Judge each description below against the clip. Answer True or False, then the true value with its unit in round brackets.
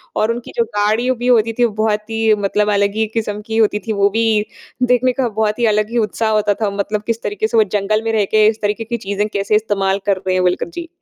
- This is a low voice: False (215 Hz)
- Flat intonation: True (1.6 semitones)